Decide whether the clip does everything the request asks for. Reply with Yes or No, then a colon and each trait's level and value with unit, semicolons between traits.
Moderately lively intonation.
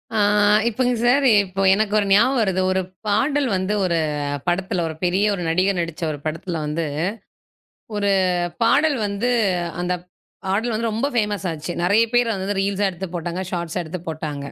Yes: average, 3.9 semitones